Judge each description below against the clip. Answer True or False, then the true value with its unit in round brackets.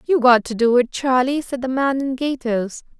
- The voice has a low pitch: False (255 Hz)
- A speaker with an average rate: False (220 wpm)